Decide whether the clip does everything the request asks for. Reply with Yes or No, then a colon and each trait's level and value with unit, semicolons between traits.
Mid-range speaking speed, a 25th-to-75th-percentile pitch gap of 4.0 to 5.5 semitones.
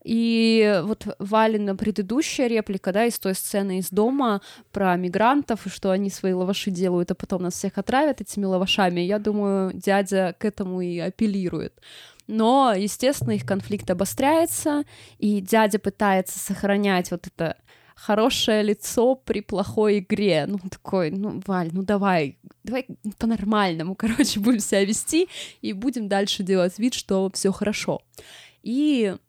No: average, 145 wpm; average, 2.7 semitones